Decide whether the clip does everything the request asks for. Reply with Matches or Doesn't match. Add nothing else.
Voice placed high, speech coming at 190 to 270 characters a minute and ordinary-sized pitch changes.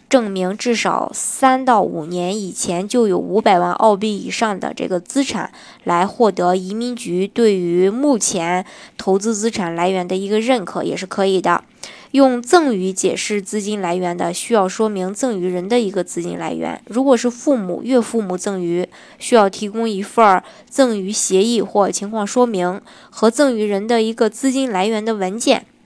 Matches